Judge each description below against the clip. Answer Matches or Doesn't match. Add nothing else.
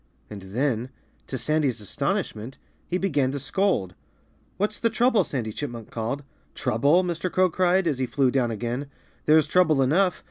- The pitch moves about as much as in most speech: Doesn't match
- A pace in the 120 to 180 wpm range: Matches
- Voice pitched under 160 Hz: Matches